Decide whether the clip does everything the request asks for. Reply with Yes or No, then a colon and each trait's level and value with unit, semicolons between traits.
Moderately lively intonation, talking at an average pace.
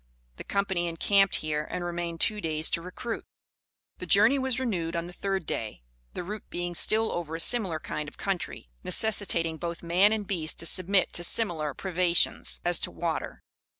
Yes: average, 3.1 semitones; average, 180 wpm